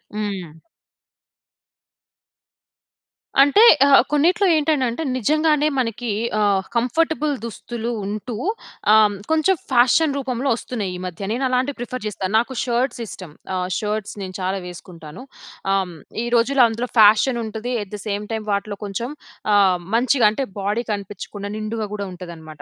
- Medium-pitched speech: No, high, 220 Hz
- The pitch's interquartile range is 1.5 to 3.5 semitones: No, average, 4.4 semitones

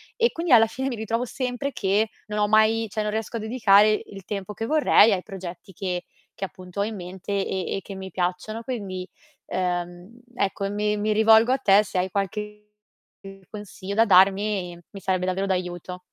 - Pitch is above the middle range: Yes, high, 205 Hz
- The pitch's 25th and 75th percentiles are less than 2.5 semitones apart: No, average, 2.8 semitones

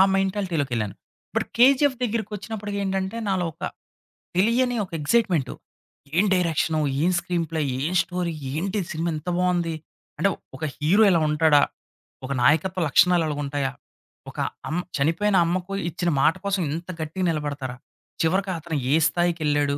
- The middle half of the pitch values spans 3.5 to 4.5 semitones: Yes, average, 3.8 semitones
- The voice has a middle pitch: Yes, medium, 175 Hz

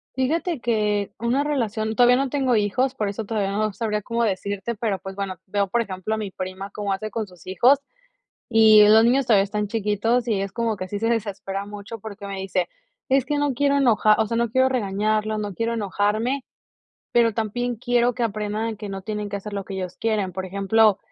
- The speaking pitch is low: No, high, 215 Hz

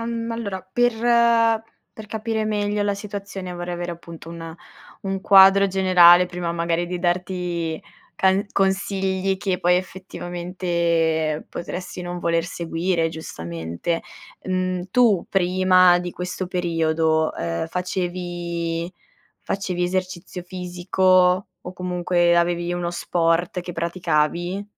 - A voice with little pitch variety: Yes, narrow, 1.8 semitones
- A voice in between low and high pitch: Yes, medium, 180 Hz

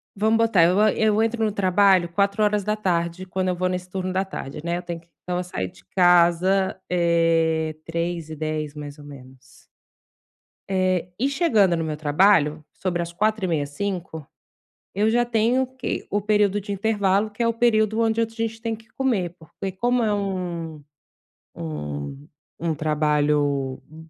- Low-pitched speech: No, medium, 185 Hz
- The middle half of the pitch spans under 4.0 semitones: No, average, 4.7 semitones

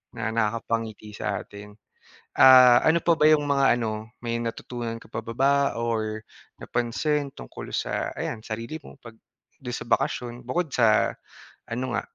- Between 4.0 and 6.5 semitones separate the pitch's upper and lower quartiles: No, average, 3.1 semitones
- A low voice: Yes, low, 120 Hz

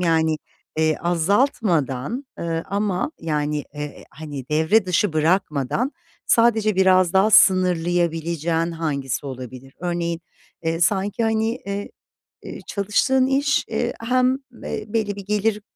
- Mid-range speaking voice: Yes, medium, 180 Hz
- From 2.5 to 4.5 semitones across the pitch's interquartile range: No, average, 5.0 semitones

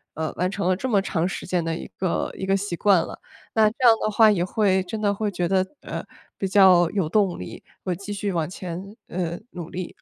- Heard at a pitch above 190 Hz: No, medium, 185 Hz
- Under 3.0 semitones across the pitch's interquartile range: Yes, narrow, 2.6 semitones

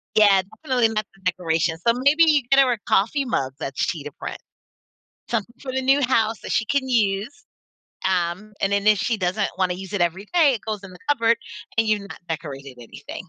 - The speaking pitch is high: Yes, high, 215 Hz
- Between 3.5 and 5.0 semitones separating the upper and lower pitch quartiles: No, wide, 5.5 semitones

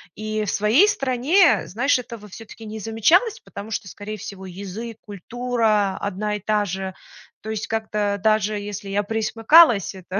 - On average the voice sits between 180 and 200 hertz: No, high, 215 Hz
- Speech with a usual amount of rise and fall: No, narrow, 2.2 semitones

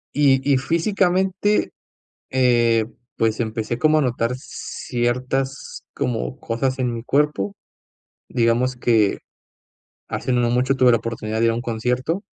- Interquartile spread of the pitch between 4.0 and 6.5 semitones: No, average, 2.8 semitones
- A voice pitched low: Yes, low, 125 Hz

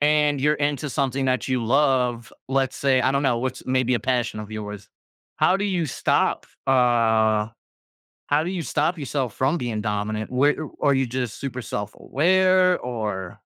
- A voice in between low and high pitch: No, low, 130 Hz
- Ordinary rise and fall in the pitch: Yes, average, 4.1 semitones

